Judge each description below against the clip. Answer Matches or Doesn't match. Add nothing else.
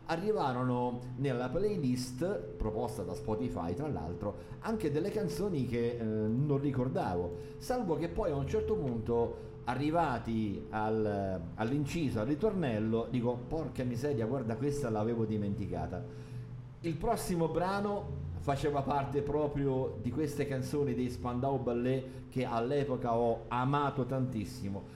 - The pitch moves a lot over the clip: Doesn't match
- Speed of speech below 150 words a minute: Matches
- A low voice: Matches